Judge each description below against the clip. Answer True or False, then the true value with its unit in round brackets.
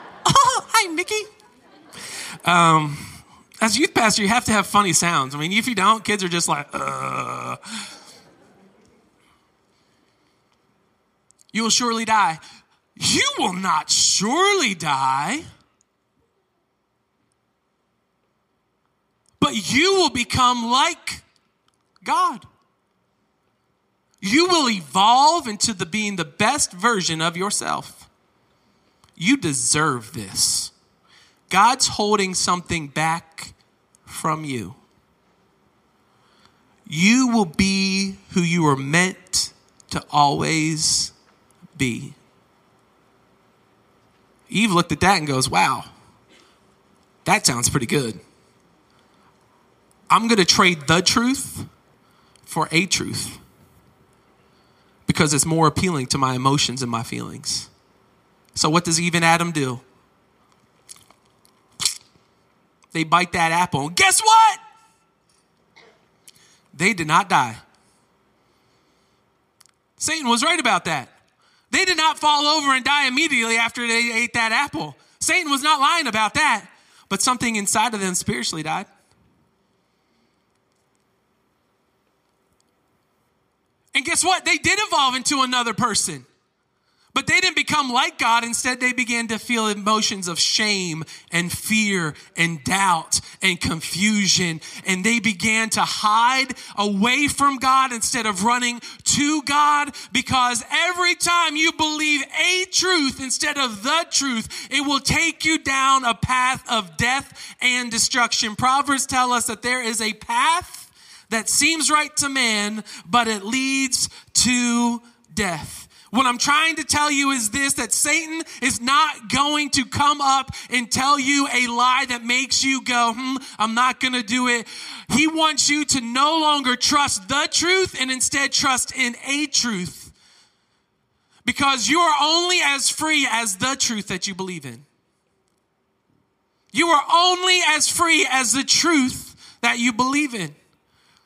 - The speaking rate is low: True (125 wpm)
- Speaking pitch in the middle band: False (240 Hz)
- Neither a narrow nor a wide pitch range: False (6.9 semitones)